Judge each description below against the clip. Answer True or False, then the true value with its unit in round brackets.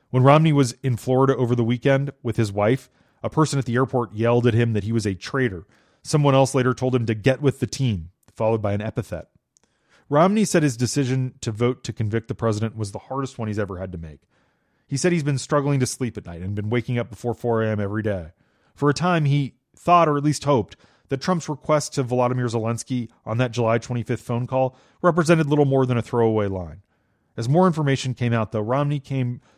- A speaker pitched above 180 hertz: False (125 Hz)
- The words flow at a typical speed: False (225 wpm)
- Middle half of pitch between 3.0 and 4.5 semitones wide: True (3.7 semitones)